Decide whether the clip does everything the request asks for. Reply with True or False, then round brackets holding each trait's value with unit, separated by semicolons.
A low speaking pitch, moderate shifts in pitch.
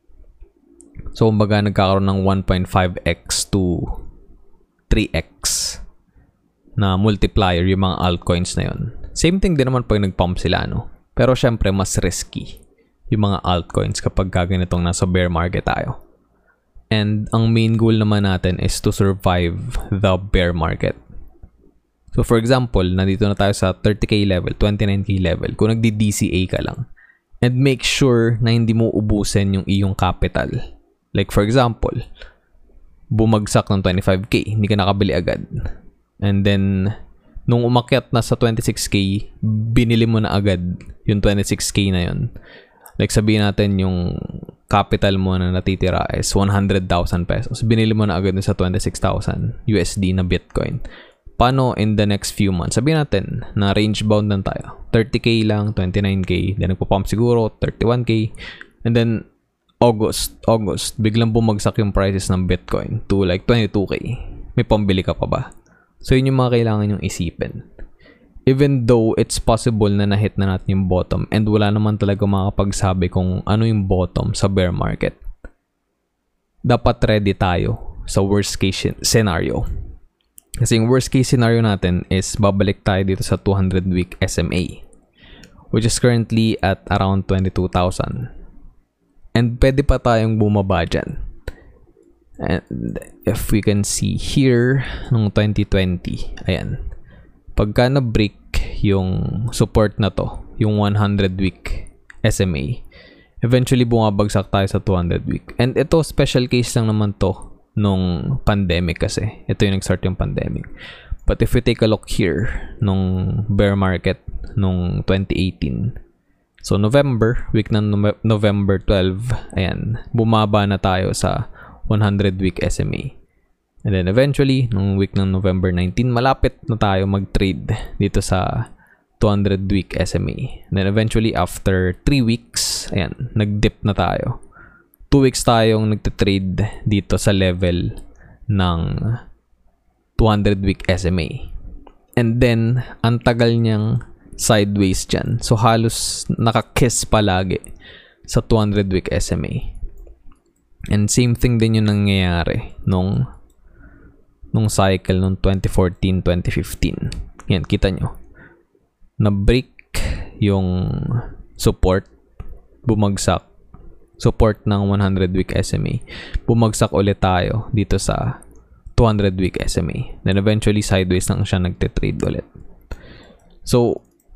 True (100 Hz; 3.3 semitones)